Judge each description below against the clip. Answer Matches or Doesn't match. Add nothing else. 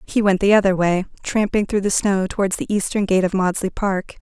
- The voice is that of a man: Doesn't match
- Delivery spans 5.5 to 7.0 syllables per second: Matches